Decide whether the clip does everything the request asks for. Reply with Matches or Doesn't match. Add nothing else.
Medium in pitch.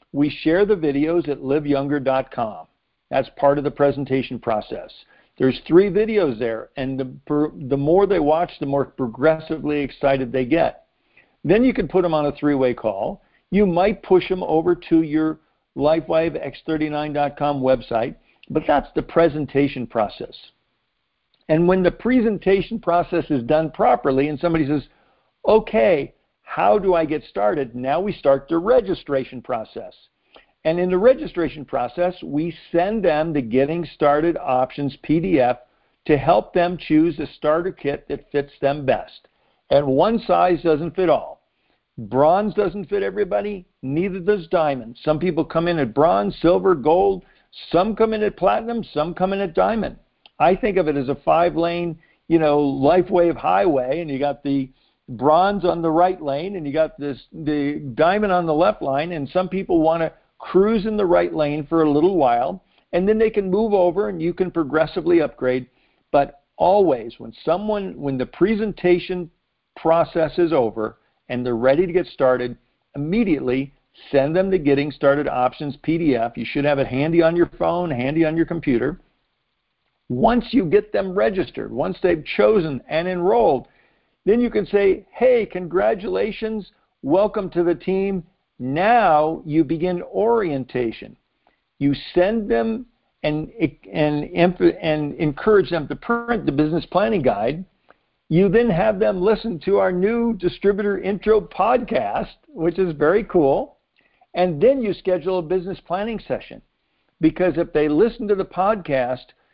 Matches